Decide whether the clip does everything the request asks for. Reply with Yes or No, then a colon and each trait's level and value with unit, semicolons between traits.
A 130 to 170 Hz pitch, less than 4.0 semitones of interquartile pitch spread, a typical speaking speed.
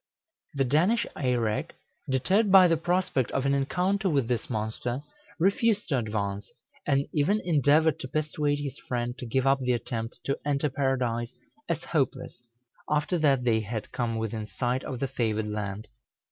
No: low, 135 Hz; average, 4.4 semitones; average, 160 wpm